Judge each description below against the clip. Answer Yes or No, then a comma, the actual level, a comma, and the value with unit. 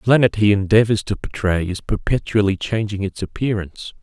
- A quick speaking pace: No, average, 165 wpm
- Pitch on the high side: No, low, 105 Hz